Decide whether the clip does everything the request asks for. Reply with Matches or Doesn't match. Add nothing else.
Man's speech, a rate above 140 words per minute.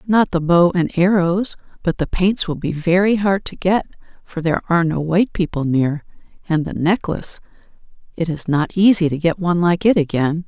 Doesn't match